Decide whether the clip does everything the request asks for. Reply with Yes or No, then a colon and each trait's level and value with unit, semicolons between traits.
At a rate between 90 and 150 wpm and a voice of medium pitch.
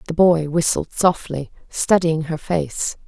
Yes: slow, 135 wpm; medium, 160 Hz